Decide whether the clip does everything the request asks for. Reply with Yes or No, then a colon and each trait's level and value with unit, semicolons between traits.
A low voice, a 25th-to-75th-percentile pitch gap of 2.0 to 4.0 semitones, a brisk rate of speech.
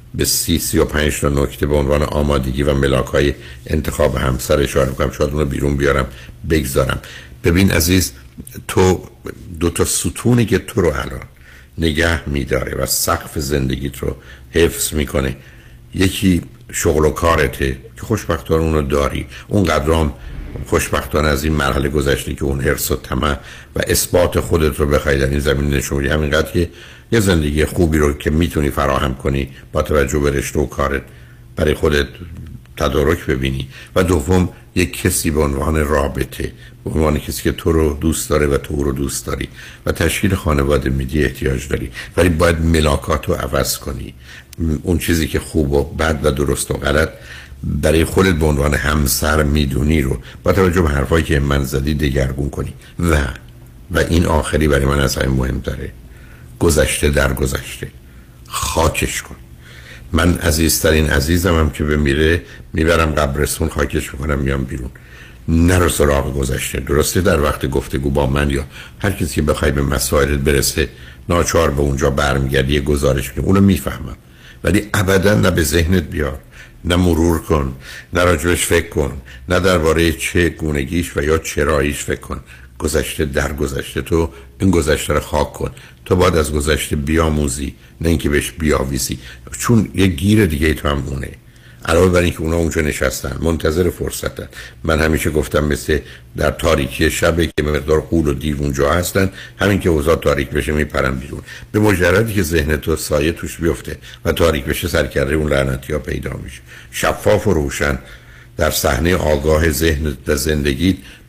Yes: very low, 75 Hz; average, 3.3 semitones; fast, 160 wpm